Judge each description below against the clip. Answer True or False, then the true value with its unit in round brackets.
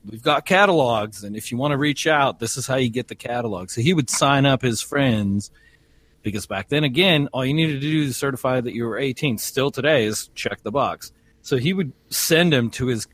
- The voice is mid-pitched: False (130 Hz)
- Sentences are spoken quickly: True (235 wpm)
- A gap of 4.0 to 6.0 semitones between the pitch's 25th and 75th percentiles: True (4.6 semitones)